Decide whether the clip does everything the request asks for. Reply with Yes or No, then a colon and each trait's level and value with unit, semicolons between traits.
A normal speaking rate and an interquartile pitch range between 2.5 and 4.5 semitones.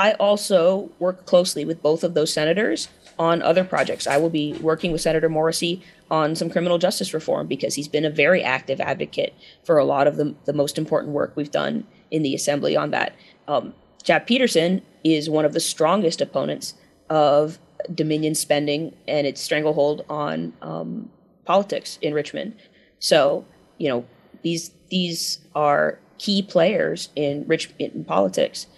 Yes: average, 165 wpm; average, 3.0 semitones